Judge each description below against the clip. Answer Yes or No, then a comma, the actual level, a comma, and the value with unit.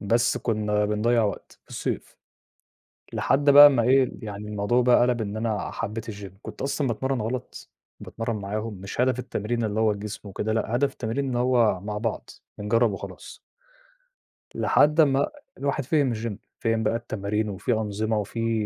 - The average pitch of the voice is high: No, low, 115 Hz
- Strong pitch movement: No, average, 2.8 semitones